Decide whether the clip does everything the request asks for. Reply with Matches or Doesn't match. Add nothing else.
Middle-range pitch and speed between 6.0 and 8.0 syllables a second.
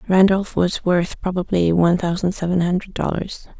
Doesn't match